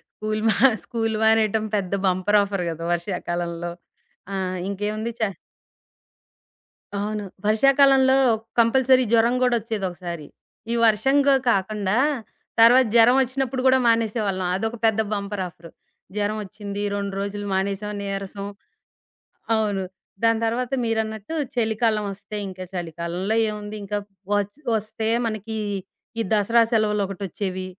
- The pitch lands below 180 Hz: No, high, 210 Hz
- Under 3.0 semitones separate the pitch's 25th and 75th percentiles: Yes, narrow, 2.5 semitones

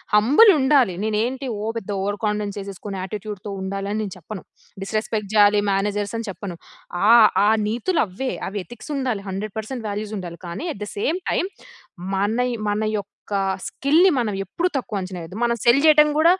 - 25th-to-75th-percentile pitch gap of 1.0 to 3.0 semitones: No, average, 3.4 semitones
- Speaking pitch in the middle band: No, high, 210 Hz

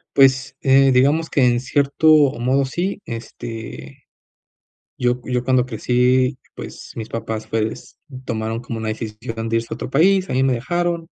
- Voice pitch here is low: Yes, low, 125 Hz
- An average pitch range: Yes, average, 3.1 semitones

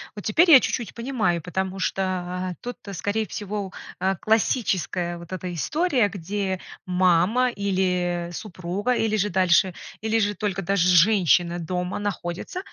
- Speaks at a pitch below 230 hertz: Yes, high, 190 Hz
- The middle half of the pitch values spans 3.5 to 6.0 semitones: No, average, 3.0 semitones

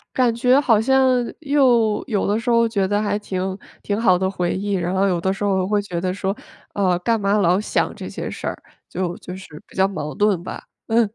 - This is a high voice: Yes, high, 200 Hz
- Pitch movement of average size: Yes, average, 3.2 semitones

